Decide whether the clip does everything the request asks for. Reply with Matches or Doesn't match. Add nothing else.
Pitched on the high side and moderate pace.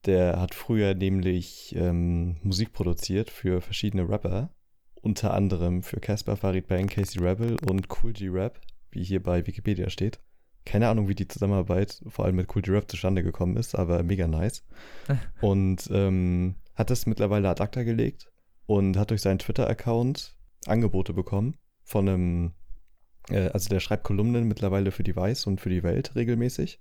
Doesn't match